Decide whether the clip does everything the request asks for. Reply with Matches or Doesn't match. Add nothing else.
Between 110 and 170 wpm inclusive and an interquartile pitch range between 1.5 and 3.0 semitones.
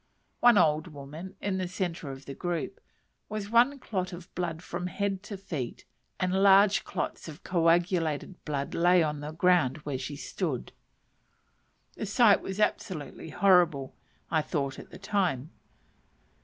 Doesn't match